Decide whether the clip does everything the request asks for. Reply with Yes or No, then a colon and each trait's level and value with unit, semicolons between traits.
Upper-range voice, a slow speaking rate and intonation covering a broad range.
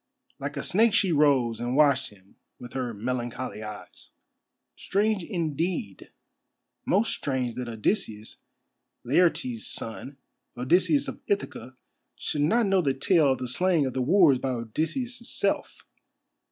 No: medium, 140 Hz; slow, 130 wpm; wide, 6.9 semitones